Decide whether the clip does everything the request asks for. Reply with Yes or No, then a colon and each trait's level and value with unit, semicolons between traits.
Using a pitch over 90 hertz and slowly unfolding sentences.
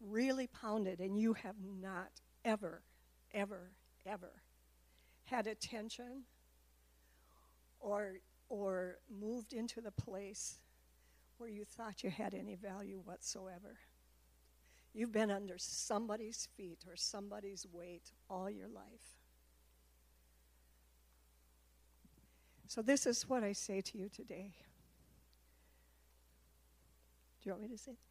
Yes: medium, 185 Hz; slow, 110 wpm